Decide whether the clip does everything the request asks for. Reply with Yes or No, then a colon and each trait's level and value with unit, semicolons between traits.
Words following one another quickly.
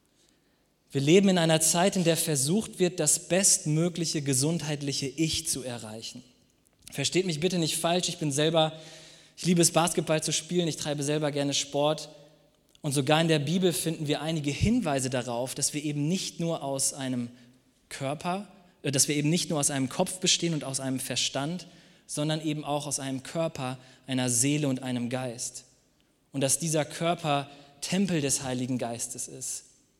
No: average, 170 wpm